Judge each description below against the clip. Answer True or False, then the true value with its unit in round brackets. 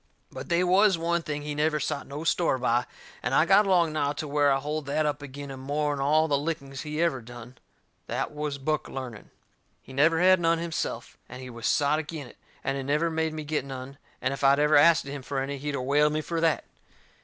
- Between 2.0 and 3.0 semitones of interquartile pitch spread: True (2.6 semitones)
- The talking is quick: True (235 wpm)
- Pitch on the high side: False (150 Hz)